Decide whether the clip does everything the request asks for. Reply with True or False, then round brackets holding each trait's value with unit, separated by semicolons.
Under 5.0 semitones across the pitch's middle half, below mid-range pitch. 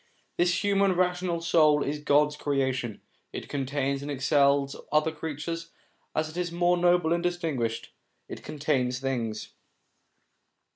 False (3.9 semitones; 150 Hz)